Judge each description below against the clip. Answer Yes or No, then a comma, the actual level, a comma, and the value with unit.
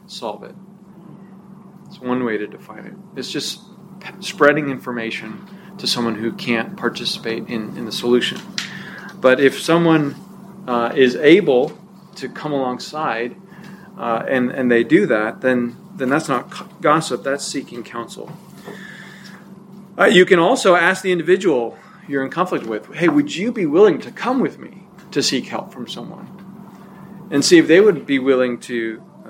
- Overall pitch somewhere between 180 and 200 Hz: Yes, medium, 185 Hz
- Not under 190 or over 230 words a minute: No, average, 160 wpm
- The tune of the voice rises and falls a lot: Yes, wide, 6.6 semitones